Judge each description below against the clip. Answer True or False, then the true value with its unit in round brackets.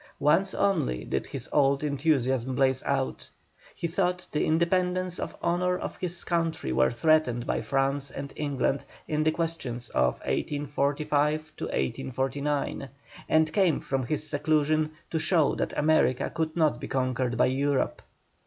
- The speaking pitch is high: False (145 Hz)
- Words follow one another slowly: False (145 wpm)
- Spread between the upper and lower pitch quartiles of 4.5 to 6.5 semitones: False (3.3 semitones)